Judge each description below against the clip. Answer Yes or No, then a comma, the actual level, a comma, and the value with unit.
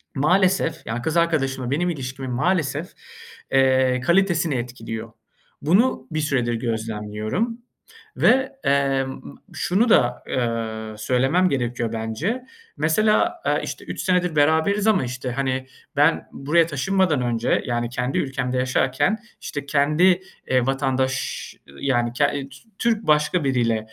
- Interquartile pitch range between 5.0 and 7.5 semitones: Yes, wide, 5.6 semitones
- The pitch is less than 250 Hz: Yes, low, 135 Hz